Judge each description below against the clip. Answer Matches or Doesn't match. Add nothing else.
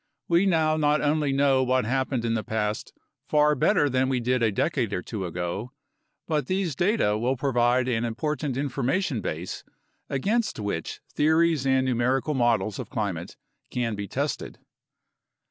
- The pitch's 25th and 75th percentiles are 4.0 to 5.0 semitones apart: Matches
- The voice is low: Matches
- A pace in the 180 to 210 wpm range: Doesn't match